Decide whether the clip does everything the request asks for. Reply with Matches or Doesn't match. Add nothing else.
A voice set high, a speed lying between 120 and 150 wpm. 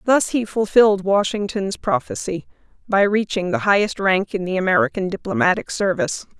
Matches